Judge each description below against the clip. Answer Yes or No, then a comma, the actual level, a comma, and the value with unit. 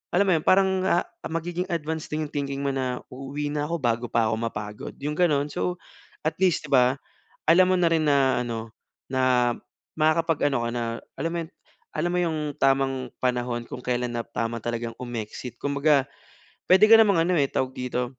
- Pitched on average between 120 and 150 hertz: Yes, medium, 140 Hz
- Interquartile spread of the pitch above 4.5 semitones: Yes, average, 4.9 semitones